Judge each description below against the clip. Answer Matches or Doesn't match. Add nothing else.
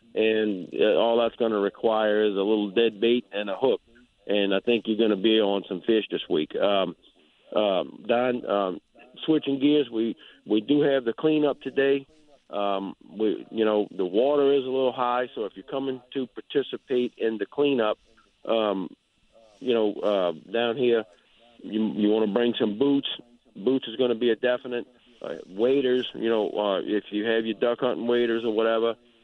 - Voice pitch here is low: Matches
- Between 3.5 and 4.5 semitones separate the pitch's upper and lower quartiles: Doesn't match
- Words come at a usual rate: Matches